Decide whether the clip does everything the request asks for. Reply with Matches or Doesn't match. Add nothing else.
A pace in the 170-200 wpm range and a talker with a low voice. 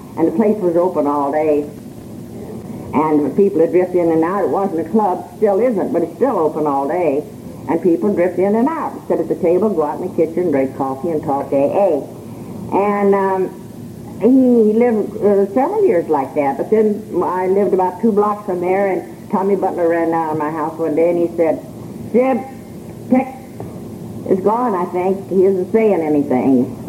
Doesn't match